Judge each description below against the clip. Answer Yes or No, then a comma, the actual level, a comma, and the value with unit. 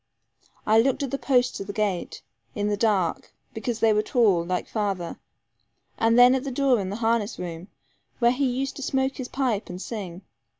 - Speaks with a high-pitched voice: Yes, high, 225 Hz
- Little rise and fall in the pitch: No, average, 4.2 semitones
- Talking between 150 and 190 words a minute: No, average, 200 wpm